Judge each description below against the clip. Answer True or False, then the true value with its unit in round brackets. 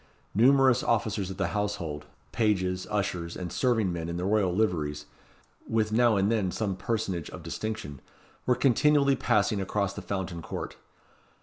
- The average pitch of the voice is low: True (100 Hz)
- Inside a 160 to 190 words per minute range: False (150 wpm)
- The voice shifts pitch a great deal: False (3.8 semitones)